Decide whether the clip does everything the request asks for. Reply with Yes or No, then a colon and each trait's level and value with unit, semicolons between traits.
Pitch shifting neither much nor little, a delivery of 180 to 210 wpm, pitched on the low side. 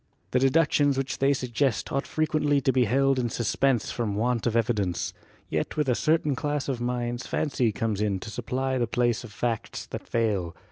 Yes: average, 3.1 semitones; average, 190 wpm; low, 125 Hz